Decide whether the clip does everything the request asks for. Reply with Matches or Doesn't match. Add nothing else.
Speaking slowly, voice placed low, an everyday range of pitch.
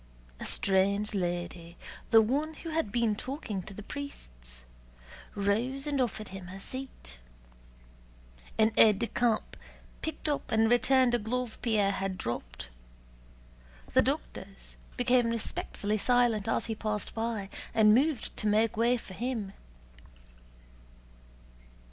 Doesn't match